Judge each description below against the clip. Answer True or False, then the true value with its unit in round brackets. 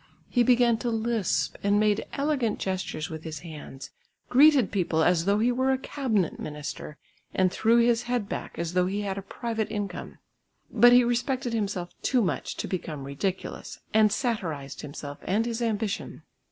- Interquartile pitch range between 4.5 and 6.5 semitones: True (5.1 semitones)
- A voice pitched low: False (210 Hz)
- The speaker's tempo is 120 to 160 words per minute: False (170 wpm)